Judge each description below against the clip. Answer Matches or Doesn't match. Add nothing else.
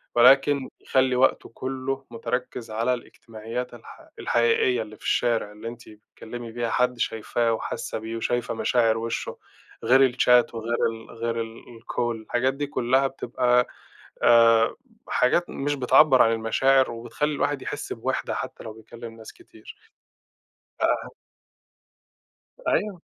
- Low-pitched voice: Matches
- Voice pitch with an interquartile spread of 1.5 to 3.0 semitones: Matches